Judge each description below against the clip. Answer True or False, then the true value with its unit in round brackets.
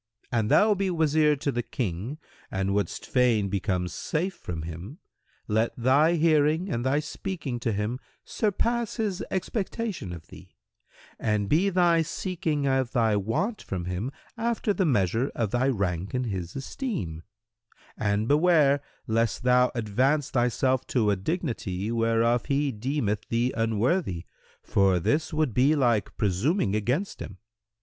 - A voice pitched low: True (125 Hz)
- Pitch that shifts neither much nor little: False (7.0 semitones)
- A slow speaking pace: False (145 wpm)